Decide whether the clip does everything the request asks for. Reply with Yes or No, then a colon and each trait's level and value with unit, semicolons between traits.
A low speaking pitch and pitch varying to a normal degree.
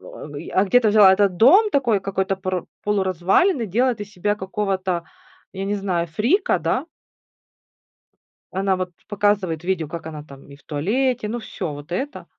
No: high, 195 Hz; average, 3.3 semitones